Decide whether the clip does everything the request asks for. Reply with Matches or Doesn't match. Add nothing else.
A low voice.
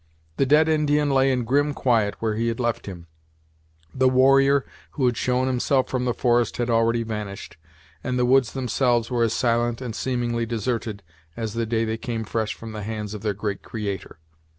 Matches